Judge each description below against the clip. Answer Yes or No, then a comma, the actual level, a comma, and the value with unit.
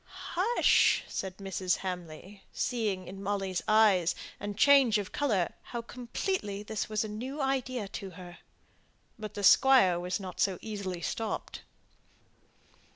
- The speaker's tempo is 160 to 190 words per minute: No, slow, 135 wpm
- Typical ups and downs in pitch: Yes, average, 4.0 semitones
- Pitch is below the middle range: No, high, 205 Hz